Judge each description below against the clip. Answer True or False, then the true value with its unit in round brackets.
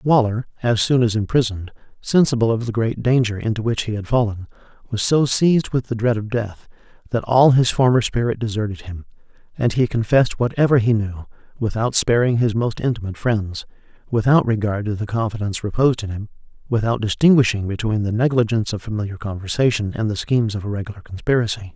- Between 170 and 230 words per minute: True (180 wpm)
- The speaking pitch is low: True (115 Hz)